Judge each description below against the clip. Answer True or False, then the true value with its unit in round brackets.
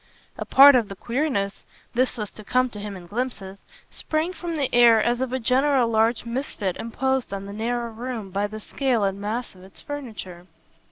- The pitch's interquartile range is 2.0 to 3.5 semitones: False (4.2 semitones)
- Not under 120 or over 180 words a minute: False (200 wpm)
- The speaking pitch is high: True (235 Hz)